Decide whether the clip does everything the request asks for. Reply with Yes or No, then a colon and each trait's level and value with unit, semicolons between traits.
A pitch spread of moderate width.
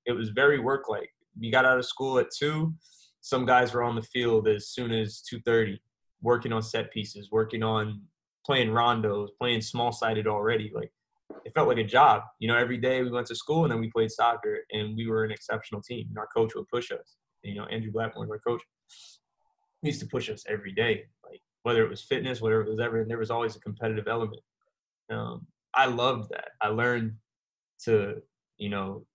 No: narrow, 2.0 semitones